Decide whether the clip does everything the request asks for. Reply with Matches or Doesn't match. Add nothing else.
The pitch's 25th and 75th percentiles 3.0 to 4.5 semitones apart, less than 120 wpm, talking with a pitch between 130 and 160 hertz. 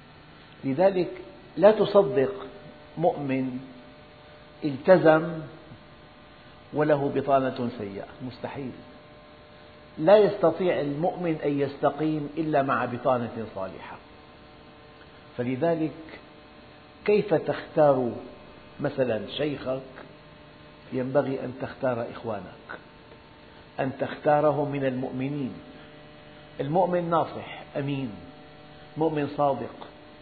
Matches